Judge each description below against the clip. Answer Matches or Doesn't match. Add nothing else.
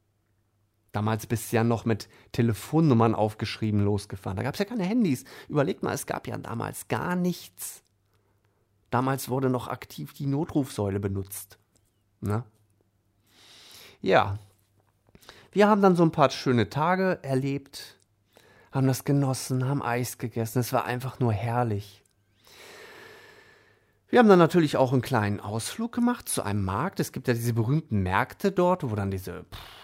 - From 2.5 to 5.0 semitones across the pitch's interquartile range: Doesn't match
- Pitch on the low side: Matches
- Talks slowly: Doesn't match